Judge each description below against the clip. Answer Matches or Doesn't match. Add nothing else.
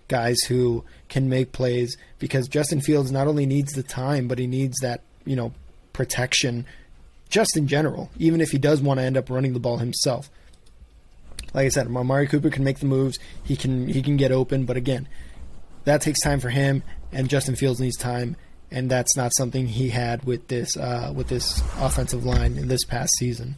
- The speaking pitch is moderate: Doesn't match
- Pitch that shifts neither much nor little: Doesn't match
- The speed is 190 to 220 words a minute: Matches